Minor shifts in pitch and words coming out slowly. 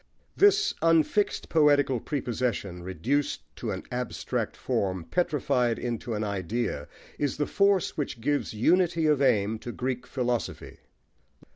No: average, 5.3 semitones; slow, 125 wpm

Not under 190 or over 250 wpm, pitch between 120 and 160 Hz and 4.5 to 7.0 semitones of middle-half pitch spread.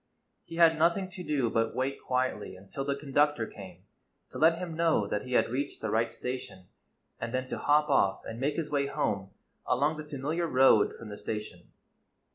Yes: average, 195 wpm; low, 135 Hz; average, 5.2 semitones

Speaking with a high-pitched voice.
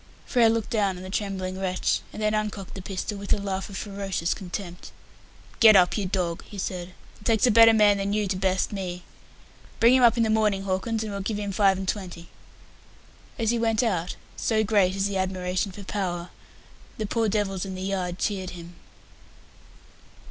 Yes: high, 195 Hz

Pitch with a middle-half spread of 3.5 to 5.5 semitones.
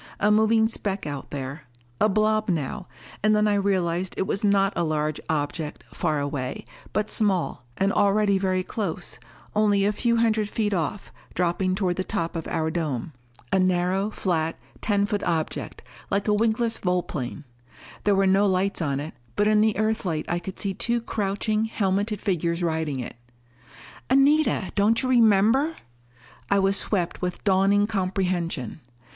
Yes: average, 3.8 semitones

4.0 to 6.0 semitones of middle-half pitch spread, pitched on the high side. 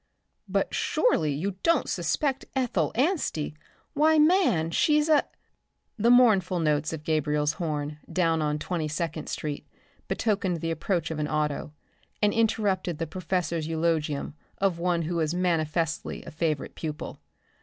No: average, 4.6 semitones; medium, 165 Hz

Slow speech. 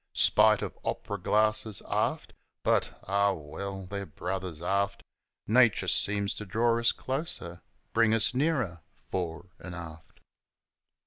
Yes: slow, 125 wpm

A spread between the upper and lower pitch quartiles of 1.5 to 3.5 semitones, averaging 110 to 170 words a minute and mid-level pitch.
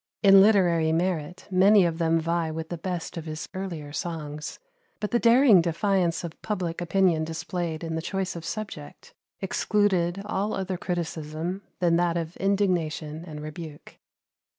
Yes: average, 3.0 semitones; average, 150 wpm; medium, 175 Hz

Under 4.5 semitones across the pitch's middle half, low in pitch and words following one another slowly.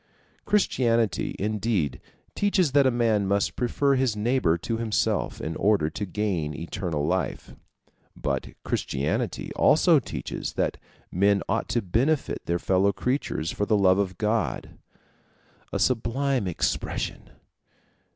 No: average, 4.9 semitones; low, 105 Hz; slow, 125 wpm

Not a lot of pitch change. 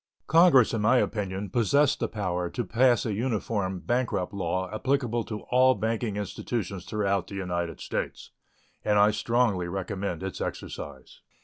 No: average, 4.1 semitones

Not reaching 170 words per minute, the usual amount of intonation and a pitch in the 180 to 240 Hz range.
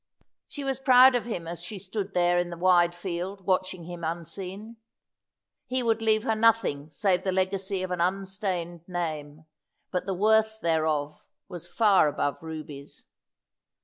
Yes: average, 155 wpm; average, 3.8 semitones; medium, 185 Hz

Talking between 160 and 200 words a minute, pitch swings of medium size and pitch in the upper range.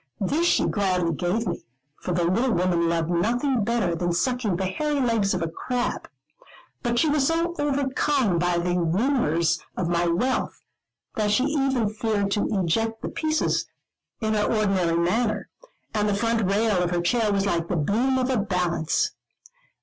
No: average, 170 wpm; wide, 5.8 semitones; high, 205 Hz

